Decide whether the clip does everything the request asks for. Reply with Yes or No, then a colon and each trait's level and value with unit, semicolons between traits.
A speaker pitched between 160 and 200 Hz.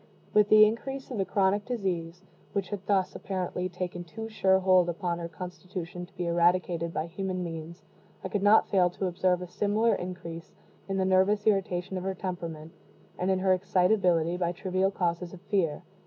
Yes: medium, 185 Hz